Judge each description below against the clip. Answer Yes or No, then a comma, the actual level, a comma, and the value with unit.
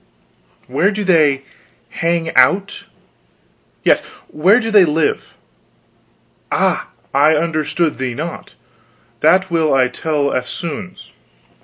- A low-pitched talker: No, medium, 160 Hz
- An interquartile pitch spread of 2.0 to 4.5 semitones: Yes, average, 4.0 semitones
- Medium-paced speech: No, slow, 105 wpm